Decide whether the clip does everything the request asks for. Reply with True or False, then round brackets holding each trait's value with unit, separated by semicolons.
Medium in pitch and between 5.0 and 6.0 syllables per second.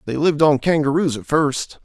True (150 Hz; 5.4 syllables/s)